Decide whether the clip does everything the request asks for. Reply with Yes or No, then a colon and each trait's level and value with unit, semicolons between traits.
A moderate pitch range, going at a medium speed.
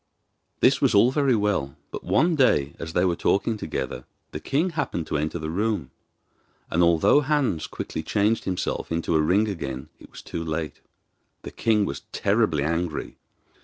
No: wide, 6.1 semitones; average, 170 wpm